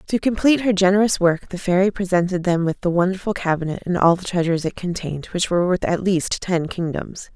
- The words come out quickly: Yes, fast, 210 wpm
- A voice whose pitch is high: No, medium, 180 Hz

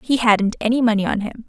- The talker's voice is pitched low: No, high, 225 Hz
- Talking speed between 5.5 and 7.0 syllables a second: Yes, 6.0 syllables/s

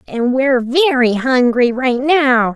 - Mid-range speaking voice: No, very high, 255 Hz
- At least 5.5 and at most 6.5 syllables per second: No, 3.8 syllables/s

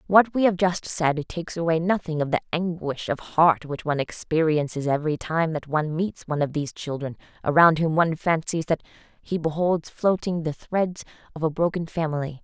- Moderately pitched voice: Yes, medium, 160 Hz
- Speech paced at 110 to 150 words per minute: No, average, 190 wpm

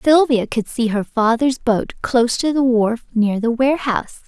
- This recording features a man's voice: No, female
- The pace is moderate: Yes, average, 185 wpm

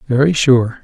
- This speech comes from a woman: No, male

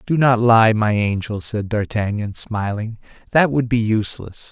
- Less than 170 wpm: Yes, average, 160 wpm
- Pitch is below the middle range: Yes, low, 110 Hz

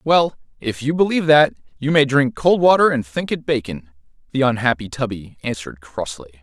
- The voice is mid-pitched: Yes, medium, 150 Hz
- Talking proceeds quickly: No, average, 175 wpm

